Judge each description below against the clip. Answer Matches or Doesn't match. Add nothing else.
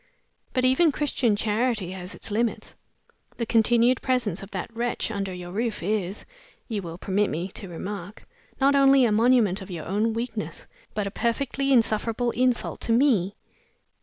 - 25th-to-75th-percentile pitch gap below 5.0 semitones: Matches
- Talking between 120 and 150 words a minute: Doesn't match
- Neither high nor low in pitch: Doesn't match